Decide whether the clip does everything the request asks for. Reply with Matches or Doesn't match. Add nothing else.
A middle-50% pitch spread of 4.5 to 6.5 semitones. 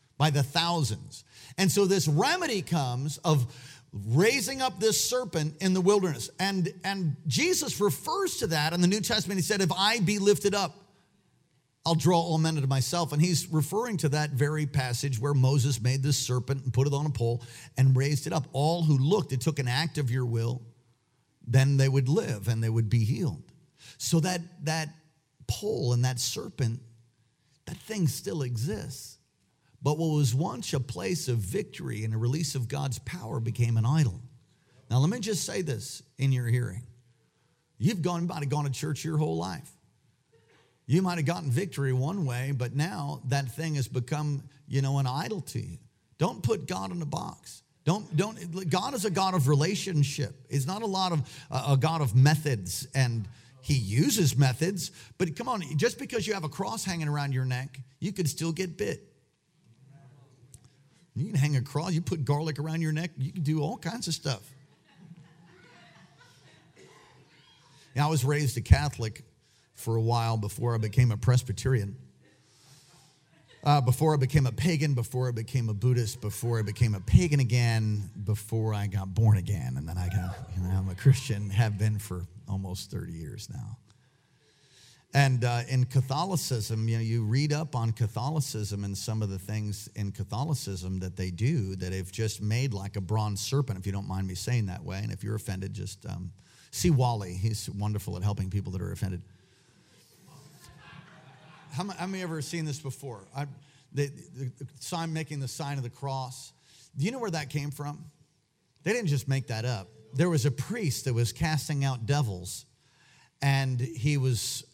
Matches